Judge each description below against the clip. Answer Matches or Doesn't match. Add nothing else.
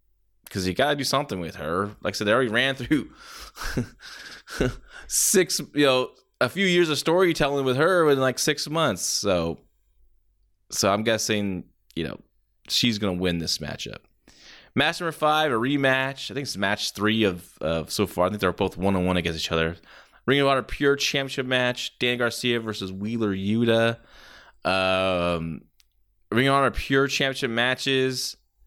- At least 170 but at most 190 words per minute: Matches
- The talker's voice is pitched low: Matches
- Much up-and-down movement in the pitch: Matches